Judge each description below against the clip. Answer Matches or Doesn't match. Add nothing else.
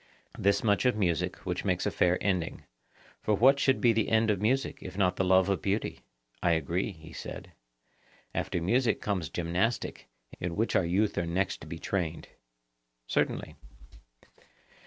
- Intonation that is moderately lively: Matches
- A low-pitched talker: Matches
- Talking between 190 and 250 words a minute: Doesn't match